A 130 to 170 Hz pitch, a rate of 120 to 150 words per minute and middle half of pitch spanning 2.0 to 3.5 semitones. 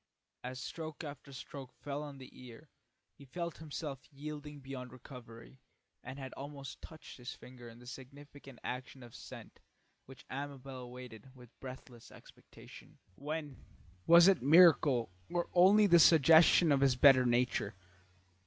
Yes: low, 135 Hz; average, 145 wpm; average, 3.0 semitones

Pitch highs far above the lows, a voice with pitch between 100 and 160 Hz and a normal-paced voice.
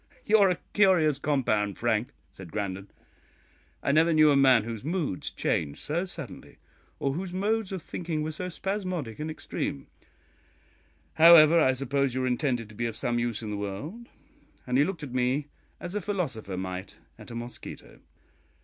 Yes: wide, 6.6 semitones; medium, 140 Hz; average, 175 wpm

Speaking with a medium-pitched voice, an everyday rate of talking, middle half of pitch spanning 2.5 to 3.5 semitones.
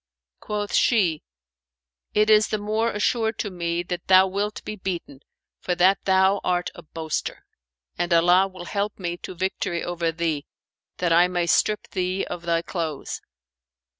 Yes: medium, 180 Hz; average, 160 wpm; average, 3.0 semitones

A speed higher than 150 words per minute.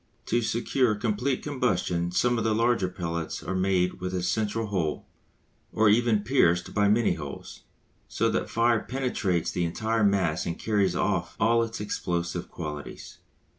Yes: average, 160 wpm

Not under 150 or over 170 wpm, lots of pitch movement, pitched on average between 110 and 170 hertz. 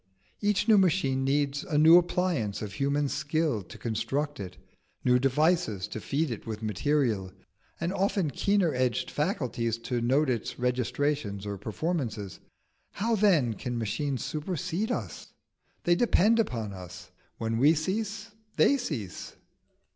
No: average, 140 wpm; wide, 7.1 semitones; medium, 140 Hz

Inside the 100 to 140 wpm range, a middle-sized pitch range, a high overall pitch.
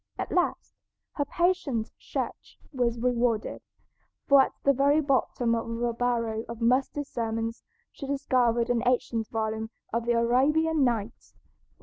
Yes: slow, 135 wpm; average, 3.1 semitones; high, 240 Hz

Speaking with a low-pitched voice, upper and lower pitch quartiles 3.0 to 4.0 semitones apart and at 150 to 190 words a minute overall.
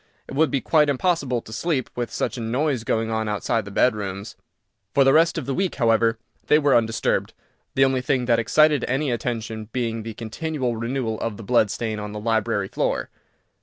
No: low, 120 Hz; average, 3.5 semitones; average, 200 wpm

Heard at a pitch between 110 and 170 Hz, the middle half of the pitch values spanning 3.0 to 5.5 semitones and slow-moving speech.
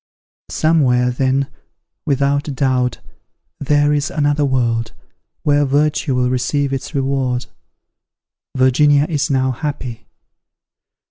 No: medium, 140 Hz; narrow, 2.4 semitones; slow, 95 wpm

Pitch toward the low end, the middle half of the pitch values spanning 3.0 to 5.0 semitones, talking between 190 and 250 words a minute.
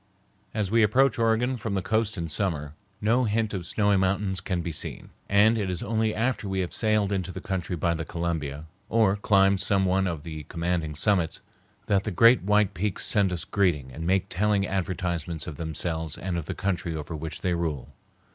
Yes: very low, 95 Hz; average, 3.8 semitones; average, 200 wpm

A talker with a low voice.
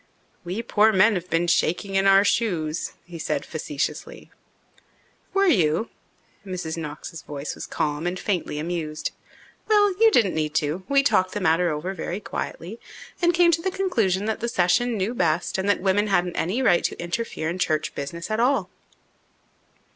No: medium, 185 Hz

